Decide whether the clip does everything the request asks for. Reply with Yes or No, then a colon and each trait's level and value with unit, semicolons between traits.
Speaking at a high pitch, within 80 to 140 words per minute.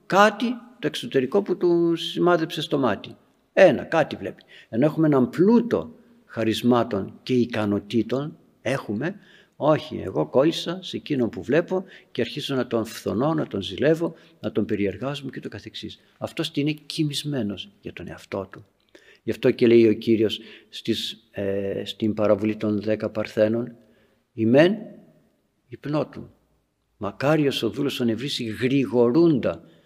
No: low, 125 Hz; average, 135 wpm